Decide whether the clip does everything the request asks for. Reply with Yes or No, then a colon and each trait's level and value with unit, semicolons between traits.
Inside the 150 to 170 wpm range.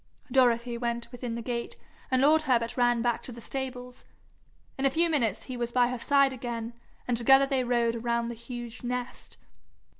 No: average, 185 wpm